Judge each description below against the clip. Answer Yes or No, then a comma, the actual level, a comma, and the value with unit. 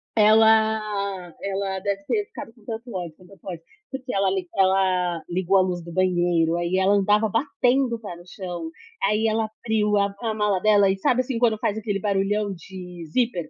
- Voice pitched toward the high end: Yes, high, 200 Hz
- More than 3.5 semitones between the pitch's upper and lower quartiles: No, average, 3.1 semitones